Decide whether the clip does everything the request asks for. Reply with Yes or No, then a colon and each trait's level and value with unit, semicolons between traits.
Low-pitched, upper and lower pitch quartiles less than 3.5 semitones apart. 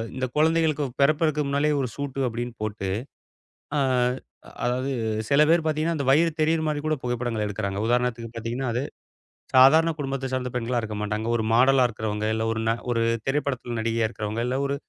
No: low, 125 Hz; average, 4.0 semitones